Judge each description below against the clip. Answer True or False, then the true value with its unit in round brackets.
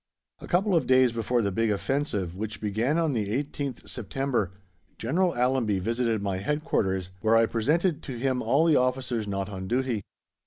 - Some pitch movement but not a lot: True (4.7 semitones)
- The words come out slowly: False (170 wpm)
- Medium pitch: False (120 Hz)